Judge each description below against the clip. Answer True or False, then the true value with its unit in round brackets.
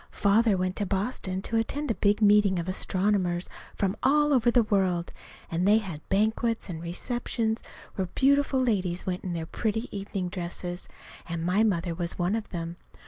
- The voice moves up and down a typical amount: True (3.9 semitones)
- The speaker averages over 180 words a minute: False (175 wpm)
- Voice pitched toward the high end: True (195 Hz)